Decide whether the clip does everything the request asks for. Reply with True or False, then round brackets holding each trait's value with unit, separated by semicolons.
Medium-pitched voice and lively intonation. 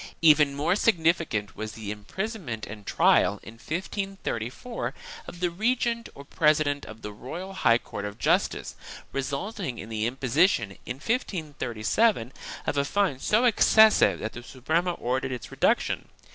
True (145 Hz; 8.7 semitones)